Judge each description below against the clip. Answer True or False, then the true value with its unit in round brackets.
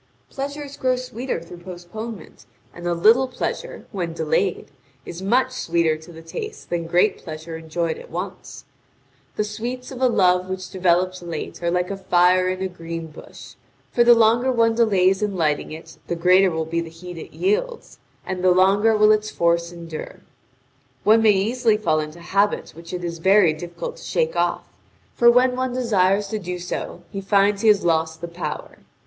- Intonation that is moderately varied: True (4.6 semitones)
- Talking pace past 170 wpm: True (185 wpm)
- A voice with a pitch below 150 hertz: False (185 Hz)